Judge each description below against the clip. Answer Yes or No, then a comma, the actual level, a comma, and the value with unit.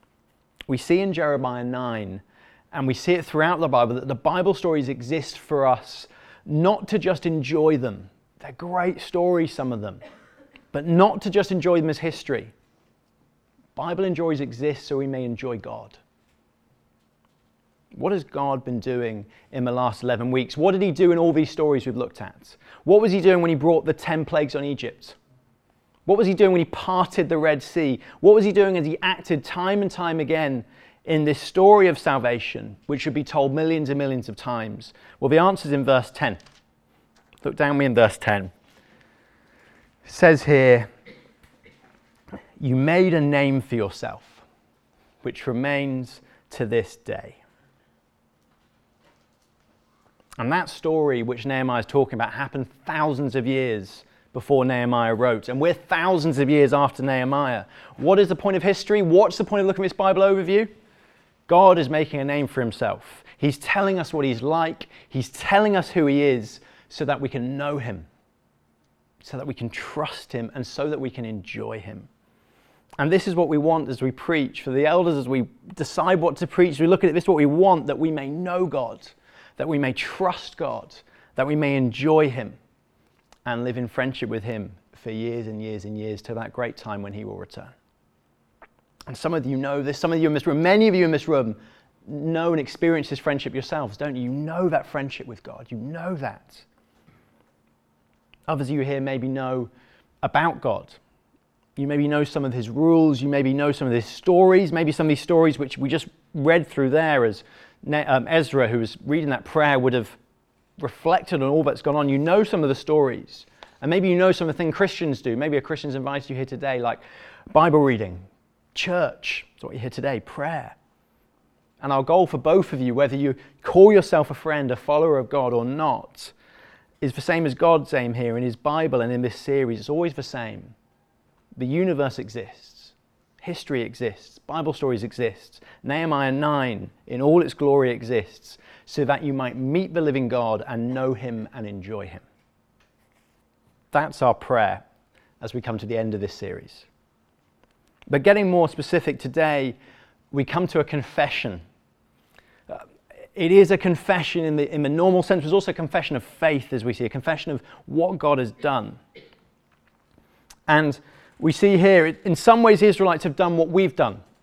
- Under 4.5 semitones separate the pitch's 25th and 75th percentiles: No, average, 4.9 semitones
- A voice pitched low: No, medium, 145 Hz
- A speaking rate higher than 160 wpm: Yes, average, 190 wpm